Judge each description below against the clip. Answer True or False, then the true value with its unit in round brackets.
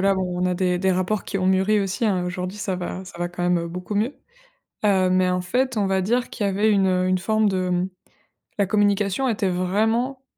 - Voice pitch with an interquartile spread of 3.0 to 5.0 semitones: False (2.4 semitones)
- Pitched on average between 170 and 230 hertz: True (190 Hz)